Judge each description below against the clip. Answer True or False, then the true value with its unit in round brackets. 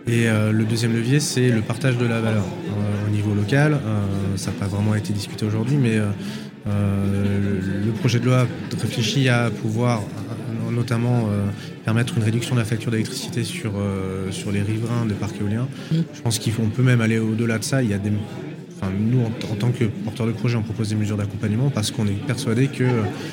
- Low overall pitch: True (110 Hz)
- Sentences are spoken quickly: False (205 wpm)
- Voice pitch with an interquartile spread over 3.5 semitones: False (2.7 semitones)